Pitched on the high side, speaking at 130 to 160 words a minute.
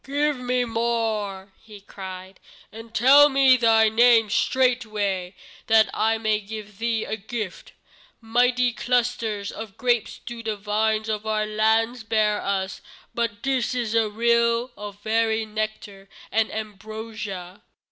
Yes: high, 220 Hz; slow, 135 wpm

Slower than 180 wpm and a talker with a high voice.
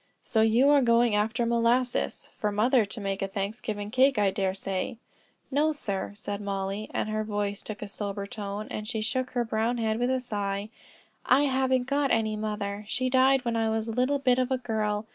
No: fast, 205 wpm; high, 220 Hz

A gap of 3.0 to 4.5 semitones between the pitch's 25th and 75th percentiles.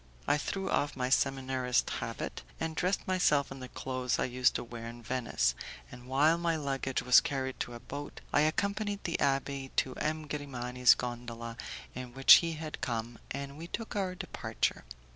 Yes: average, 3.7 semitones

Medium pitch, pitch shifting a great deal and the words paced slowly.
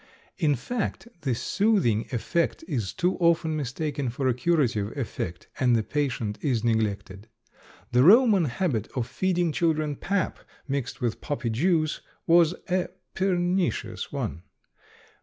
Yes: medium, 145 Hz; wide, 6.7 semitones; slow, 130 wpm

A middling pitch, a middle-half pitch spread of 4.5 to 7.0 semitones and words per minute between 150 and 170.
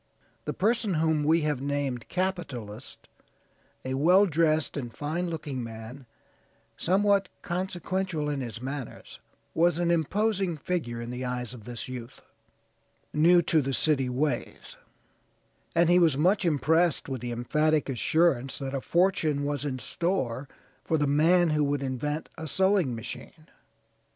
No: medium, 150 Hz; average, 4.8 semitones; average, 140 wpm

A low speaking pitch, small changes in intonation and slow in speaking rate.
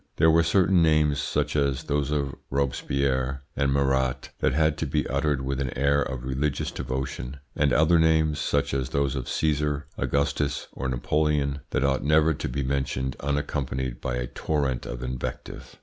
No: very low, 70 Hz; narrow, 2.2 semitones; average, 170 wpm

